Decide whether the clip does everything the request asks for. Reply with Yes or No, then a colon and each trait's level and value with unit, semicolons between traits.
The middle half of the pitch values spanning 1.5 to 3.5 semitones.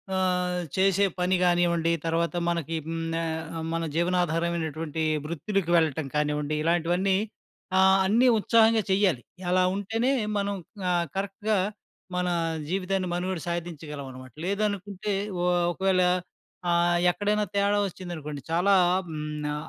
Yes: average, 2.9 semitones